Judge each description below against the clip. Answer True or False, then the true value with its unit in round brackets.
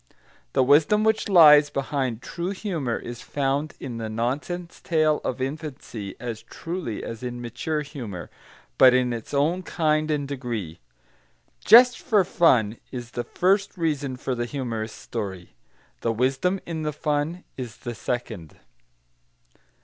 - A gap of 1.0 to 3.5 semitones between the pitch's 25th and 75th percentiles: False (5.0 semitones)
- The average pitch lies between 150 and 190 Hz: False (135 Hz)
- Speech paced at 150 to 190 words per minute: False (140 wpm)